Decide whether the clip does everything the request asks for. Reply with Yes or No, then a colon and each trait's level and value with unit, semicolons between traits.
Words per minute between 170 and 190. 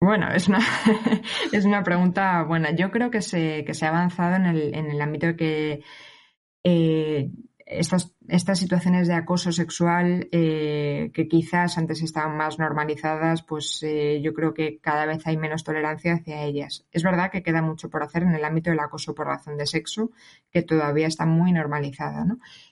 Yes: average, 185 wpm